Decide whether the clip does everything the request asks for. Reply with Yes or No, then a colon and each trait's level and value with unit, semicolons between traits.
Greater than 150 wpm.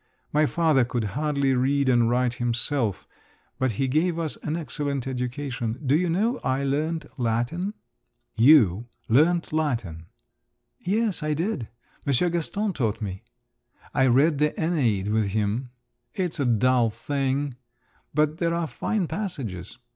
No: average, 140 wpm